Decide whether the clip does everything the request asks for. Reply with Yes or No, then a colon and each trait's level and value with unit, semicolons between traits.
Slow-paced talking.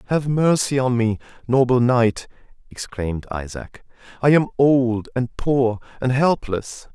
Yes: slow, 130 wpm